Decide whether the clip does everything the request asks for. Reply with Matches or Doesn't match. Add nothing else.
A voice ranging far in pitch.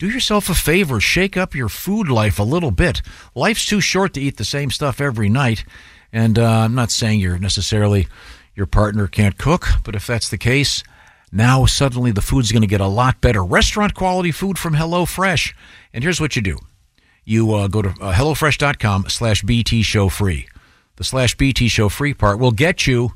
Matches